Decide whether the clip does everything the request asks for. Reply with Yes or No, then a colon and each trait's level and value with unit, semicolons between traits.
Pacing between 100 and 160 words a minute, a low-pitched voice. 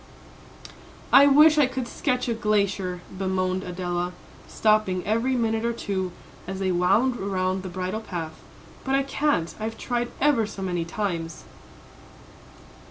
No: average, 140 wpm; high, 200 Hz